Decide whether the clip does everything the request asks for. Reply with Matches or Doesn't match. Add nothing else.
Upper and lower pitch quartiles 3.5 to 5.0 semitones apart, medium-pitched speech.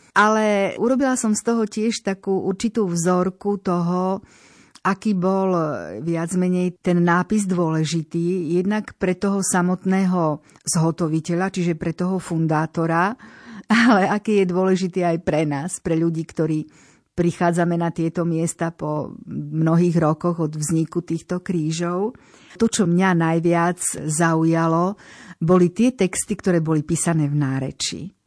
Doesn't match